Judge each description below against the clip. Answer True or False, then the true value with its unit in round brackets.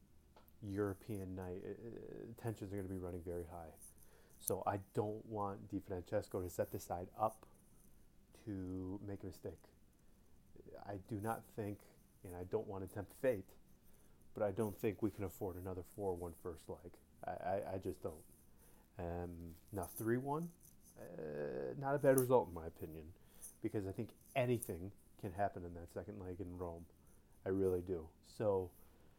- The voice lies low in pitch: True (95 Hz)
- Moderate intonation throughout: True (3.4 semitones)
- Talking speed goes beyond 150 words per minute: True (165 wpm)